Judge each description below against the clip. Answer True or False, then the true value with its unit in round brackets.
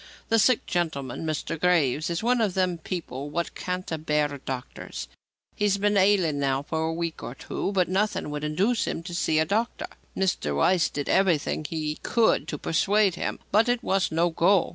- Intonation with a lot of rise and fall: False (4.5 semitones)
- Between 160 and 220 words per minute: True (185 wpm)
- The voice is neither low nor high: True (170 Hz)